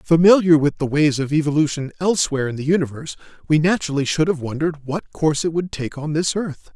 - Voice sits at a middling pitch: Yes, medium, 155 Hz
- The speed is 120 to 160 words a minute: No, fast, 205 wpm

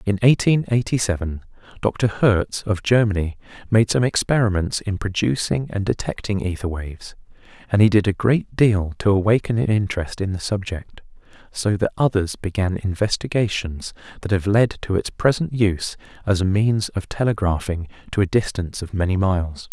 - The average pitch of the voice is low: Yes, low, 100 Hz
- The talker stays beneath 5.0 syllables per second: No, 5.1 syllables/s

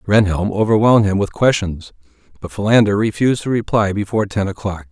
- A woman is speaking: No, male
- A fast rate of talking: No, average, 160 wpm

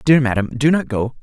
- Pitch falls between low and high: No, low, 130 Hz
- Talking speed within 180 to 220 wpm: No, fast, 245 wpm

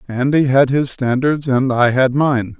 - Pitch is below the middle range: Yes, low, 130 Hz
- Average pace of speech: Yes, average, 185 wpm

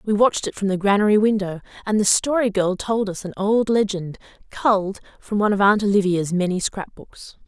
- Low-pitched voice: No, high, 200 Hz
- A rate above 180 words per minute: Yes, average, 195 wpm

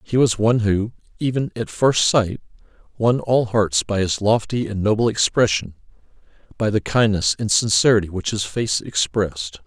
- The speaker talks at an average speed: Yes, average, 160 wpm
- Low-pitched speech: Yes, low, 105 Hz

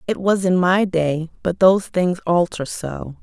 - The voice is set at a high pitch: No, medium, 180 Hz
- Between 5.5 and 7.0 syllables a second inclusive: No, 4.2 syllables/s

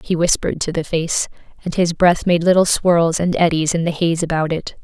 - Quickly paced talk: Yes, fast, 225 wpm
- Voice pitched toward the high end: No, medium, 170 Hz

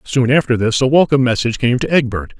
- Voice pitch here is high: No, low, 125 Hz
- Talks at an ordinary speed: No, fast, 225 wpm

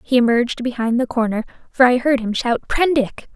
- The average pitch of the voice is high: Yes, high, 245 Hz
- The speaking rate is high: No, average, 195 wpm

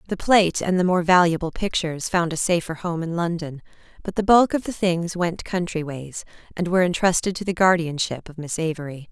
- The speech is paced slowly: No, fast, 205 wpm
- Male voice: No, female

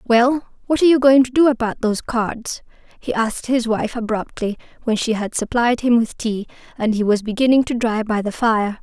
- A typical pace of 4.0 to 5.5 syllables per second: Yes, 5.4 syllables/s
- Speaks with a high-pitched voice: Yes, high, 230 Hz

